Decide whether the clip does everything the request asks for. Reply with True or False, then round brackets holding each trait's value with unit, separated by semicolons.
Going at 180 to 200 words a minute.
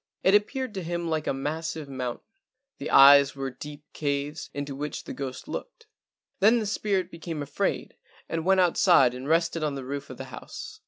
True (190 wpm)